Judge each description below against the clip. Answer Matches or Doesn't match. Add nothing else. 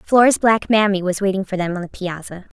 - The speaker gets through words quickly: Matches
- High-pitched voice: Matches